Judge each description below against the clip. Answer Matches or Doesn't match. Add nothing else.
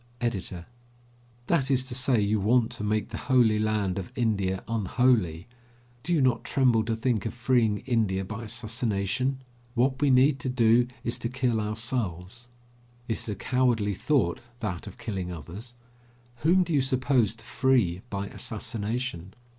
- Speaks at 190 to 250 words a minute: Doesn't match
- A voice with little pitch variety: Doesn't match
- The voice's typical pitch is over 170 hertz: Doesn't match